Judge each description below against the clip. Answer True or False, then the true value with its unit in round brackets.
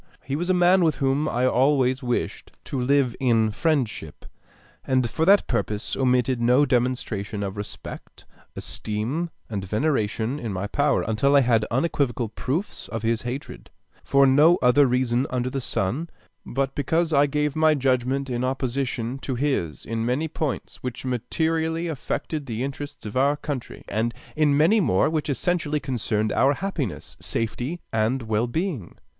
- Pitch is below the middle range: True (130 Hz)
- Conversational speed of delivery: True (160 wpm)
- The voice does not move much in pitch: False (4.0 semitones)